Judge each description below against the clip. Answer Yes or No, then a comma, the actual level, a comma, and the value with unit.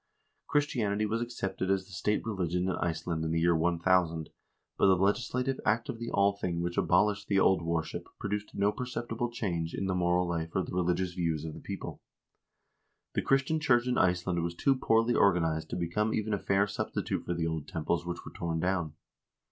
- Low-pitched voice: Yes, very low, 95 Hz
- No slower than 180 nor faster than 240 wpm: Yes, average, 195 wpm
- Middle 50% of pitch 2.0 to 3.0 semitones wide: No, average, 3.8 semitones